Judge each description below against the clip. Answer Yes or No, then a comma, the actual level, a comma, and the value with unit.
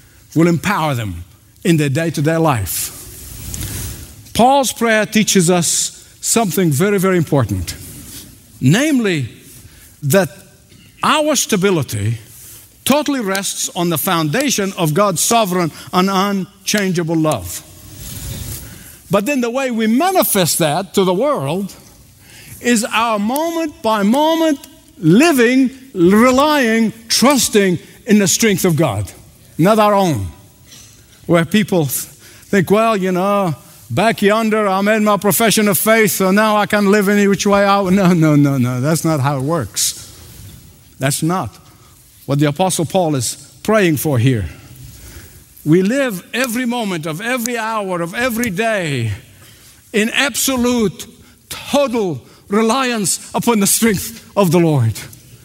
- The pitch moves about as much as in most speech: No, wide, 8.6 semitones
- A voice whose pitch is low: No, medium, 185 Hz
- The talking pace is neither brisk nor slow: No, slow, 130 wpm